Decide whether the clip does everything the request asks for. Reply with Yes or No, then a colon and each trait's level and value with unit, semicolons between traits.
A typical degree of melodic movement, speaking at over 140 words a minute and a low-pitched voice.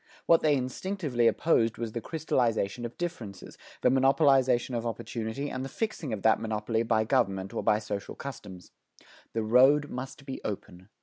Yes: average, 3.8 semitones; average, 165 wpm; low, 120 Hz